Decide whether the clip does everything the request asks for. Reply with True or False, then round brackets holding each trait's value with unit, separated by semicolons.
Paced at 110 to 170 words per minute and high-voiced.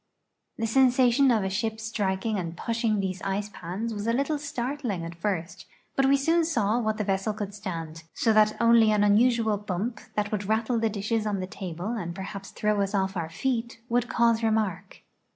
False (195 wpm; 215 Hz)